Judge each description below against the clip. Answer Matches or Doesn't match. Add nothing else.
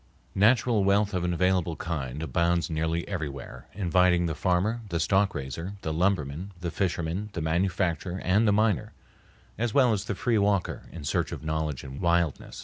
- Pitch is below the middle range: Matches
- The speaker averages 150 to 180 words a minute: Matches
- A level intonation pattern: Doesn't match